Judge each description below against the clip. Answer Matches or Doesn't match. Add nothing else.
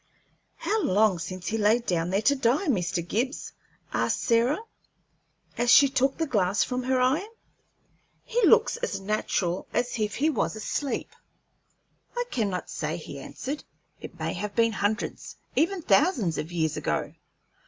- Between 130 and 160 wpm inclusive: Matches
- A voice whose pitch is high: Matches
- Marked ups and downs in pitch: Matches